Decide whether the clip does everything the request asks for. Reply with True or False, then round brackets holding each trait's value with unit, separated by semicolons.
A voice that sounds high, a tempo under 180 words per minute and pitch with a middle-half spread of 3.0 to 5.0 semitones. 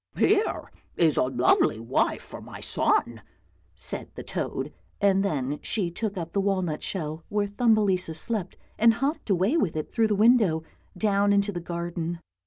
True (195 Hz; 170 wpm; 4.4 semitones)